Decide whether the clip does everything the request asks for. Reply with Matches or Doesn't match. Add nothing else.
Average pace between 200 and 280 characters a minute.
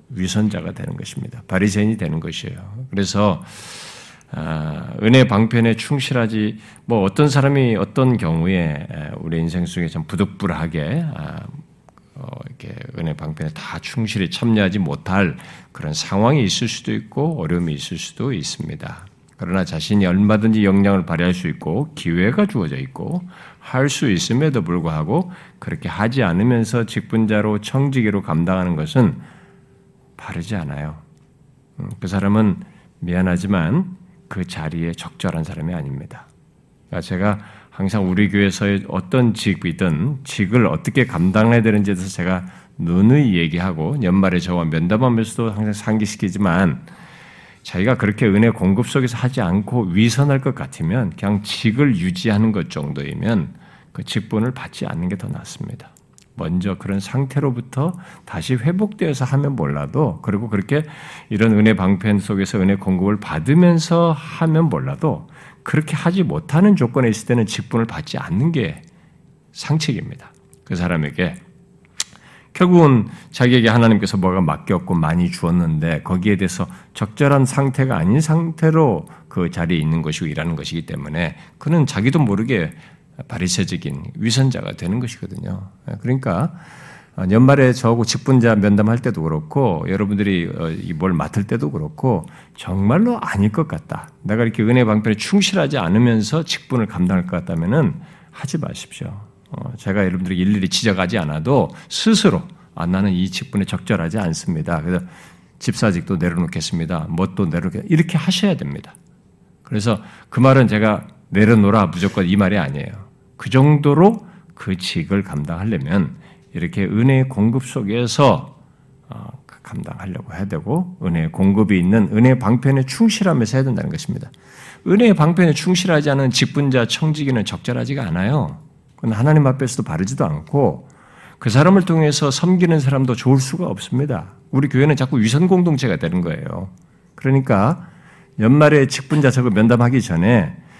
Doesn't match